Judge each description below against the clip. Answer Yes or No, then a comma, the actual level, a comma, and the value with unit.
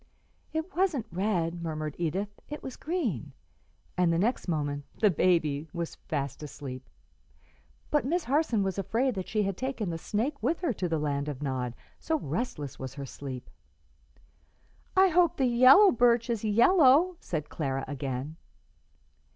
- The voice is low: No, high, 190 Hz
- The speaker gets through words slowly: No, average, 155 wpm